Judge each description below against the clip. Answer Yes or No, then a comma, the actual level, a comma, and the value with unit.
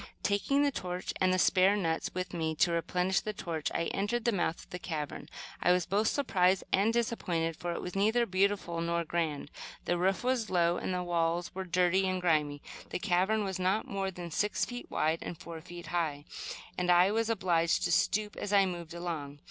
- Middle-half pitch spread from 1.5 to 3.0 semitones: Yes, average, 2.7 semitones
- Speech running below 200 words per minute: No, fast, 205 wpm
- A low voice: No, medium, 180 Hz